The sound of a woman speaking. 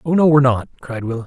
No: male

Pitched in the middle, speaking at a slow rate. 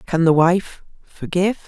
Yes: medium, 175 Hz; slow, 110 wpm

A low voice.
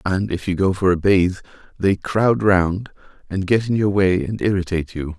Yes: very low, 95 Hz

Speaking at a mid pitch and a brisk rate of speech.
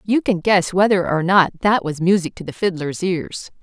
Yes: medium, 180 Hz; fast, 215 wpm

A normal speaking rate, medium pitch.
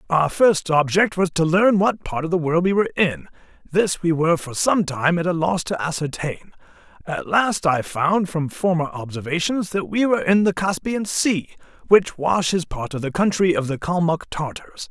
Yes: average, 195 wpm; medium, 170 Hz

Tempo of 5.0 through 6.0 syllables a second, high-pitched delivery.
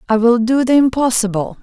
Yes: 5.6 syllables/s; high, 240 Hz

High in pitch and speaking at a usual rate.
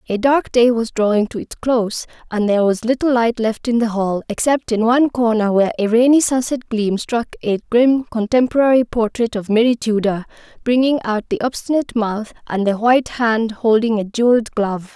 Yes: high, 230 Hz; average, 190 wpm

